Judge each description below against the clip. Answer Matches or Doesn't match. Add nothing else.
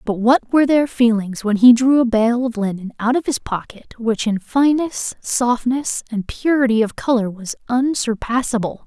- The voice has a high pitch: Matches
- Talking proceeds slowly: Doesn't match